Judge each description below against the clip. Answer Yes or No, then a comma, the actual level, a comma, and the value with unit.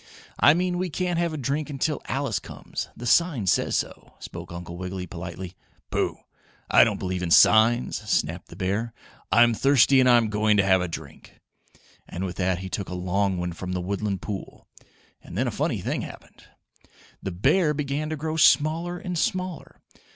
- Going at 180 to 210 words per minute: Yes, average, 185 wpm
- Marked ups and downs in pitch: Yes, wide, 8.7 semitones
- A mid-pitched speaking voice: No, low, 110 Hz